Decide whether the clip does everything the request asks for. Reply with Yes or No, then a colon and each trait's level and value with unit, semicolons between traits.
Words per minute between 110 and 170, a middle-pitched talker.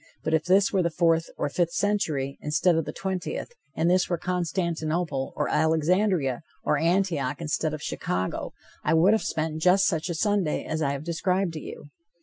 No: average, 190 wpm; medium, 165 Hz